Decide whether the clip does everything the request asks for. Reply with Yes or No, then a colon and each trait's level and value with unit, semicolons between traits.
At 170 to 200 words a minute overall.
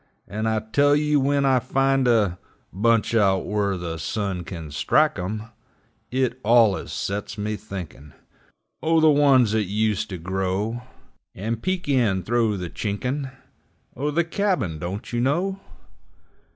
No: average, 145 wpm